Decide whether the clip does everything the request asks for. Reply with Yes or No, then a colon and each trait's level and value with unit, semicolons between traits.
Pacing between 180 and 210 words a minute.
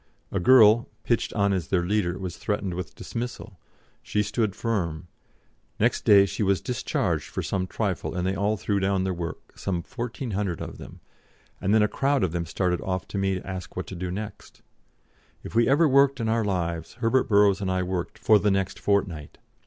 Yes: average, 200 wpm